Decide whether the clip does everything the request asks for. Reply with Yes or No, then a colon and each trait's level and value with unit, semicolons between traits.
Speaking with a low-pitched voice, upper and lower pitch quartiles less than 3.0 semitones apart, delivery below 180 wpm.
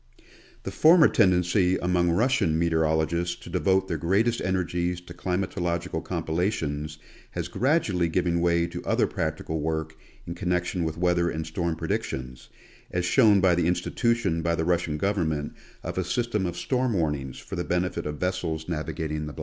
Yes: very low, 85 Hz; narrow, 2.5 semitones; average, 165 wpm